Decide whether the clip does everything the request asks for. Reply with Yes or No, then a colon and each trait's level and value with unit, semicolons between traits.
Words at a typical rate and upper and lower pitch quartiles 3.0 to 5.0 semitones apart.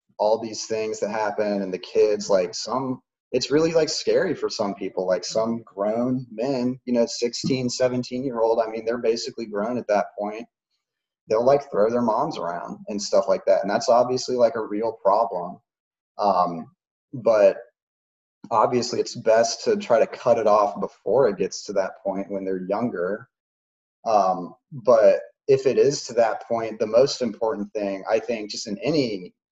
Yes: average, 180 wpm; average, 3.8 semitones